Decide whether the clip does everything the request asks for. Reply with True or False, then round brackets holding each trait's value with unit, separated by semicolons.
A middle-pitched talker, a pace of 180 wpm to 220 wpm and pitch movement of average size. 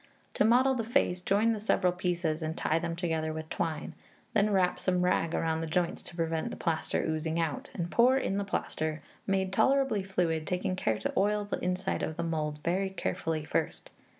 True (180 Hz; 200 wpm; 3.5 semitones)